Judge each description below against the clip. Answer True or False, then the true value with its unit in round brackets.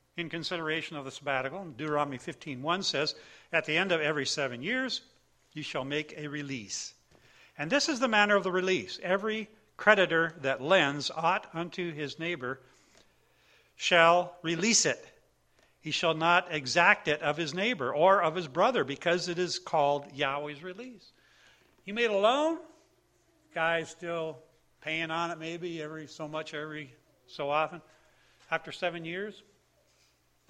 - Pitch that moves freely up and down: False (3.6 semitones)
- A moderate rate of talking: True (150 wpm)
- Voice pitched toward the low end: False (165 Hz)